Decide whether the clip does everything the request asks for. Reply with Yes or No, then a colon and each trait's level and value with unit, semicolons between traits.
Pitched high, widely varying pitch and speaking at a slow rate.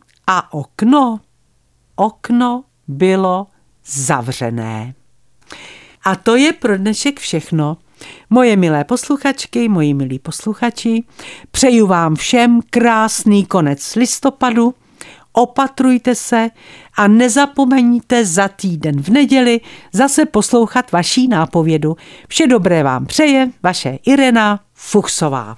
Yes: high, 215 Hz; wide, 7.3 semitones; slow, 100 wpm